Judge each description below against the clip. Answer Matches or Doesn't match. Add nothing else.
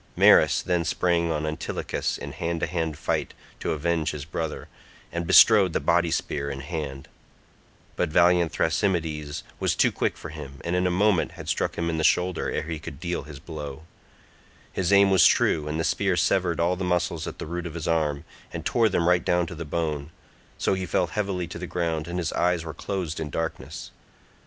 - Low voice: Matches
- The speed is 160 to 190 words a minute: Doesn't match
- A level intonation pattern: Matches